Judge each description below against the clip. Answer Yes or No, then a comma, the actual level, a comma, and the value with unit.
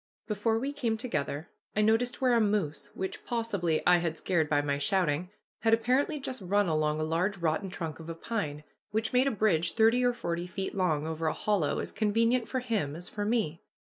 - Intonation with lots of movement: Yes, wide, 5.9 semitones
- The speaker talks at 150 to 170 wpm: No, fast, 205 wpm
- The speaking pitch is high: Yes, high, 195 Hz